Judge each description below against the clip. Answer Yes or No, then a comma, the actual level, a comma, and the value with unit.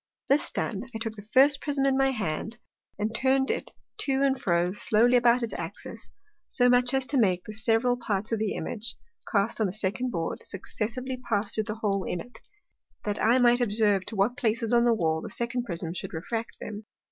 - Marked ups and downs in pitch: No, average, 3.3 semitones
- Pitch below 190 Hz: No, high, 225 Hz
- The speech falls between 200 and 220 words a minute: Yes, fast, 205 wpm